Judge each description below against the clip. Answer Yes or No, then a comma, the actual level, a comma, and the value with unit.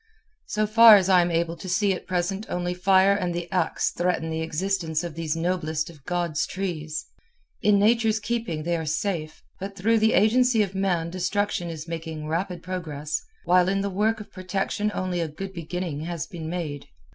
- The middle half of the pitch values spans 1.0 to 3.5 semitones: Yes, average, 3.2 semitones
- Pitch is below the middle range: No, medium, 180 Hz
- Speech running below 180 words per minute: No, average, 190 wpm